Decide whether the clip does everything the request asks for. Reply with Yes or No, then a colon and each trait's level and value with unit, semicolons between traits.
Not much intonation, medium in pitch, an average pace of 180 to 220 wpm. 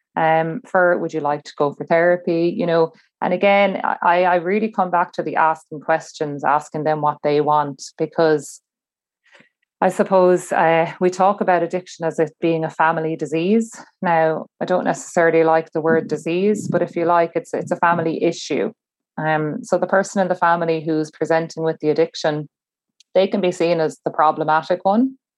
Yes: narrow, 2.3 semitones; medium, 165 Hz; average, 185 wpm